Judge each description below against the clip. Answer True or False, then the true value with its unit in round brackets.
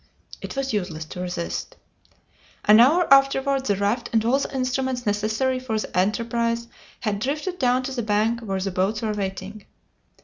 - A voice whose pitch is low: False (230 Hz)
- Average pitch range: True (4.2 semitones)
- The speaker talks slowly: False (170 wpm)